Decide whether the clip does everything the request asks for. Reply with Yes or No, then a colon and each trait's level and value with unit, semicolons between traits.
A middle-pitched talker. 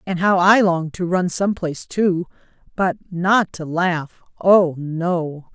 Yes: medium, 175 Hz